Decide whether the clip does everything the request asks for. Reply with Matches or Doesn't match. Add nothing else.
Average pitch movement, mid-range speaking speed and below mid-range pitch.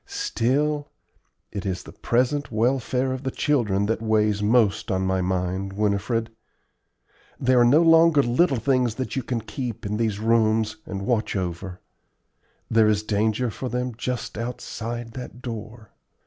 Matches